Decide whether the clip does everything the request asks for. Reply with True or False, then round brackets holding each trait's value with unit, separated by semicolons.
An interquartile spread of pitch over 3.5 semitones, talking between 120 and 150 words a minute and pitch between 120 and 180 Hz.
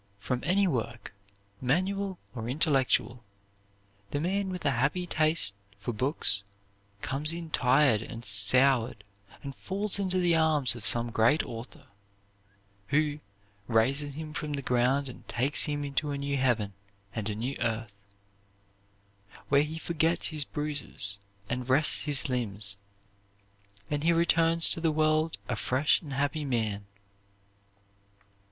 True (4.7 semitones; 135 wpm; 140 Hz)